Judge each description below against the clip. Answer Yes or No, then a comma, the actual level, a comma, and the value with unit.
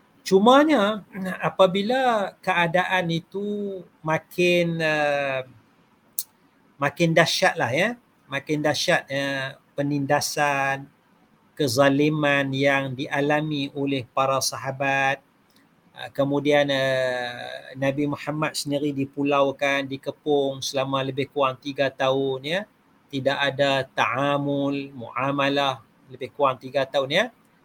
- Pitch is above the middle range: No, medium, 140 Hz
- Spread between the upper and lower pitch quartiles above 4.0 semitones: No, narrow, 2.6 semitones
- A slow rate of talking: Yes, slow, 95 wpm